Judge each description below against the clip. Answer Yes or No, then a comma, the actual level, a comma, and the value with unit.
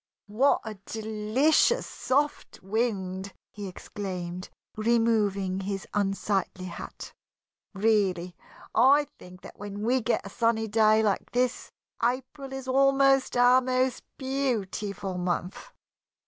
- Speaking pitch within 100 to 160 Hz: No, high, 220 Hz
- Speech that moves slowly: Yes, slow, 110 wpm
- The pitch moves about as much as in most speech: Yes, average, 4.6 semitones